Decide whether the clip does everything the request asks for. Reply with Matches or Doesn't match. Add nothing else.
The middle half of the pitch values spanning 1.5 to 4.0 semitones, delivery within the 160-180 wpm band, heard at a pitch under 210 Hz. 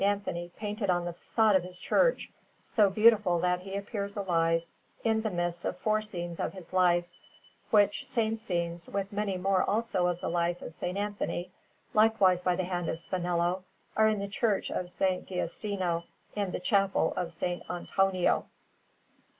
Matches